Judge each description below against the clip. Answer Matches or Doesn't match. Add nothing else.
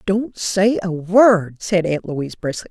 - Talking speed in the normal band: Matches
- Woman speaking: Matches